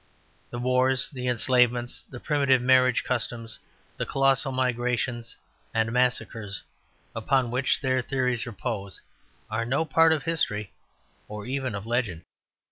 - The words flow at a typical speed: No, slow, 125 wpm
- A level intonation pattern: Yes, narrow, 2.3 semitones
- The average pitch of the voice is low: Yes, low, 125 Hz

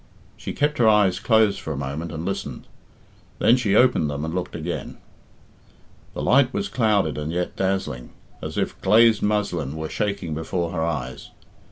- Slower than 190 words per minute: Yes, average, 170 wpm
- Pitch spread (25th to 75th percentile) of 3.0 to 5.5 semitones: Yes, average, 5.1 semitones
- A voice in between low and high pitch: No, very low, 90 Hz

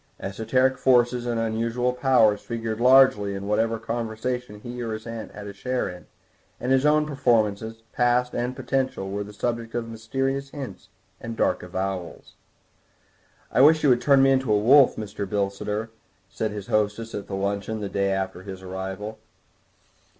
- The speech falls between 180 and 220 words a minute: No, average, 165 wpm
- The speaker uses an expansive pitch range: No, average, 3.5 semitones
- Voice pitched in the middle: No, low, 115 Hz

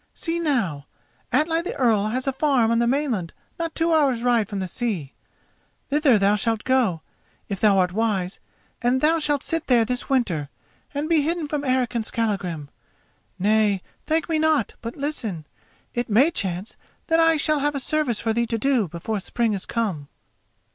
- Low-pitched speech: No, high, 240 Hz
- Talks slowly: No, average, 180 wpm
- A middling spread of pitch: No, wide, 6.1 semitones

